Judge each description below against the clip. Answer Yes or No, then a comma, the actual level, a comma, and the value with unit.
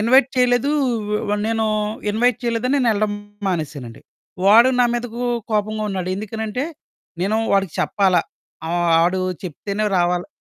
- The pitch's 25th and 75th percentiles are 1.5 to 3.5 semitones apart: No, average, 4.2 semitones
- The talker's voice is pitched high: Yes, high, 215 Hz